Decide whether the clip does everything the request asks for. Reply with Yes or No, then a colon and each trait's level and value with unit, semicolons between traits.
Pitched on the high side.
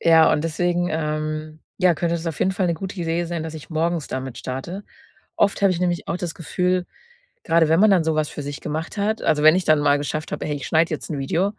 No: medium, 165 Hz